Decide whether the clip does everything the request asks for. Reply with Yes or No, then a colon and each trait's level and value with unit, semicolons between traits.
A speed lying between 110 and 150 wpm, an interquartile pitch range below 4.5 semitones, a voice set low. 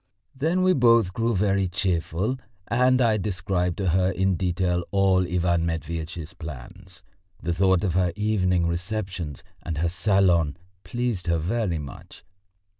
Yes: average, 140 wpm; average, 3.4 semitones; very low, 90 Hz